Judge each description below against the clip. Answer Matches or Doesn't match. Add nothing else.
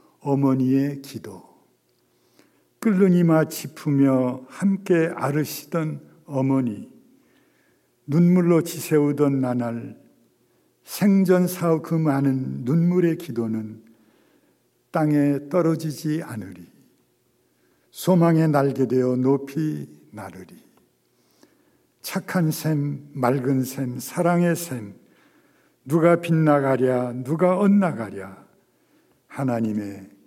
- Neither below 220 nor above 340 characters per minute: Doesn't match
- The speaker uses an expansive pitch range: Doesn't match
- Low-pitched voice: Doesn't match